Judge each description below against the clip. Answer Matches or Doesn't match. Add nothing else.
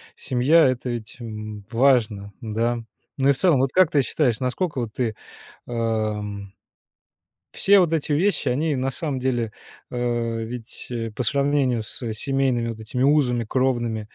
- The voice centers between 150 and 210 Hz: Doesn't match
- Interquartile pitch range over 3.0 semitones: Matches